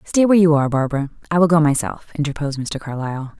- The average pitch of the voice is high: No, medium, 150 Hz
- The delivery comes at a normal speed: No, fast, 210 wpm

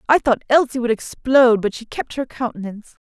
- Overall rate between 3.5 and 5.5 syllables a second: No, 5.8 syllables/s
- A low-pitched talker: No, high, 240 Hz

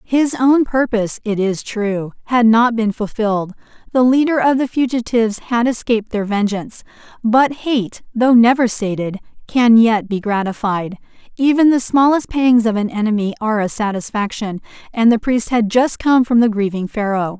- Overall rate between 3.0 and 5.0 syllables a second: Yes, 4.9 syllables/s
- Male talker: No, female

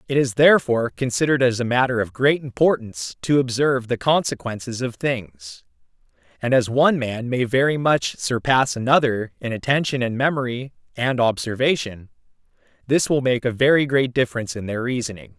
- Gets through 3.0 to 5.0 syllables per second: No, 5.5 syllables/s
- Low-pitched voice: Yes, low, 120 Hz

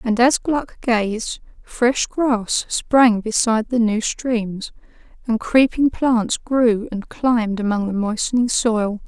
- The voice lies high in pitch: Yes, high, 230 Hz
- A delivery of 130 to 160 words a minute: Yes, average, 140 wpm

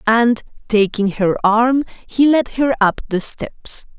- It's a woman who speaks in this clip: Yes, female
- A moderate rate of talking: Yes, average, 150 wpm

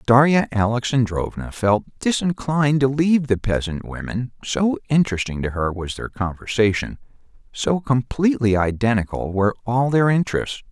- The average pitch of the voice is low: Yes, low, 120 Hz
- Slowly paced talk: Yes, slow, 130 wpm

